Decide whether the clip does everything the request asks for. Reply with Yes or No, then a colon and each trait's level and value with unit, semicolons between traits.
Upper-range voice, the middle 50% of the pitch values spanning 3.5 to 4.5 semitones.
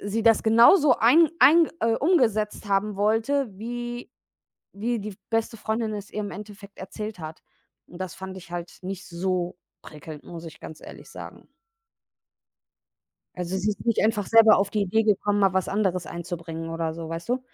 Yes: high, 205 Hz; average, 3.9 semitones